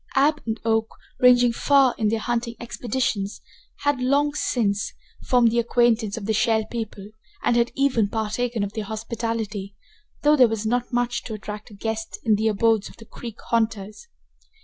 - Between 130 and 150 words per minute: No, average, 170 wpm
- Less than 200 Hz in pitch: No, high, 230 Hz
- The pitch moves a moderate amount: No, narrow, 2.2 semitones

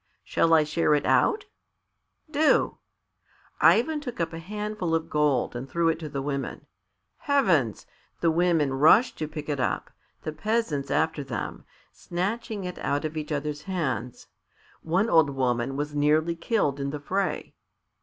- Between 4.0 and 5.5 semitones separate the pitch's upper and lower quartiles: Yes, average, 4.4 semitones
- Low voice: No, medium, 160 Hz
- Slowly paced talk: No, average, 155 wpm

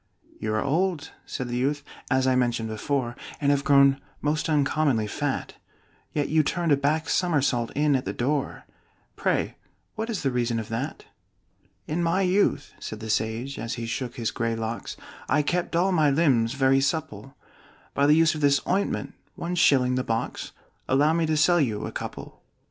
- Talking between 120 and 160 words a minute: No, average, 180 wpm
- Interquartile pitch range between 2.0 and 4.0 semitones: No, average, 4.4 semitones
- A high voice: No, medium, 140 Hz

